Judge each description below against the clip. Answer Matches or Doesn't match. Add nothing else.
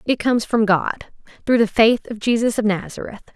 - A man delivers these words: Doesn't match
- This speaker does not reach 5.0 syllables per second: Doesn't match